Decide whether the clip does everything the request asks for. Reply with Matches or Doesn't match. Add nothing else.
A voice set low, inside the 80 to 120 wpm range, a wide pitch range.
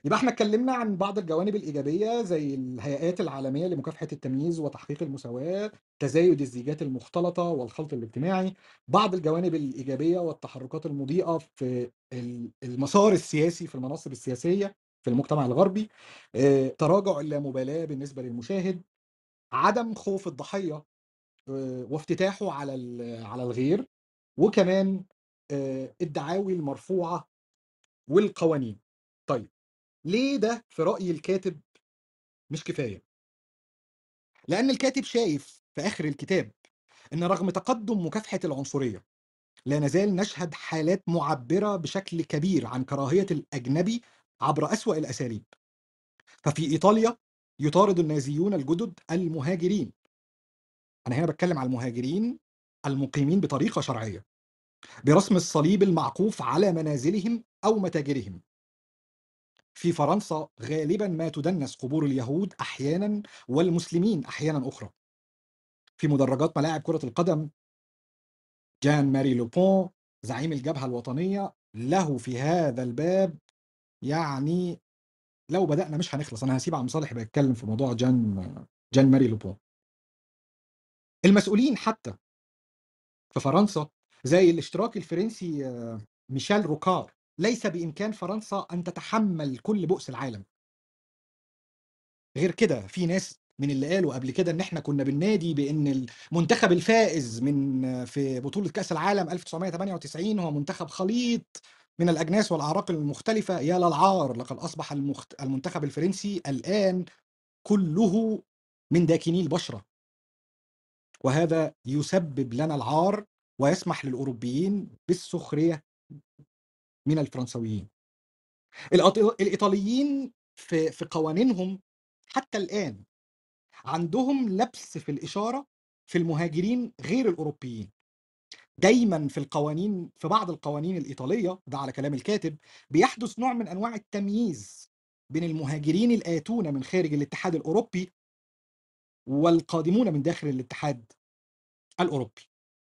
Doesn't match